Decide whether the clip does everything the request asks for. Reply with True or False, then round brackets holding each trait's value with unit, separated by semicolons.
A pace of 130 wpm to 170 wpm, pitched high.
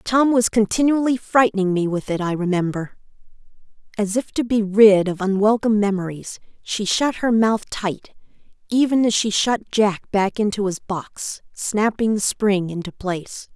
True (160 wpm; 210 Hz)